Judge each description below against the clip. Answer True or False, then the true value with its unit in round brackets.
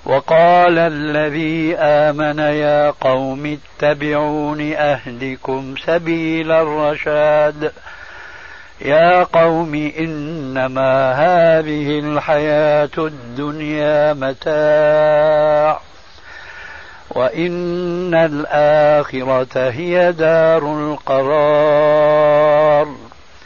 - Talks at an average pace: False (55 wpm)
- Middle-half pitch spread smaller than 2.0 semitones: True (1.5 semitones)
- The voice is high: False (150 Hz)